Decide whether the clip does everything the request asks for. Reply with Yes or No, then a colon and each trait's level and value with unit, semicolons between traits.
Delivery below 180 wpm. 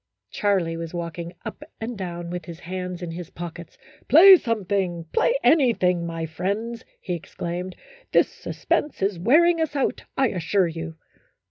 Yes: average, 160 wpm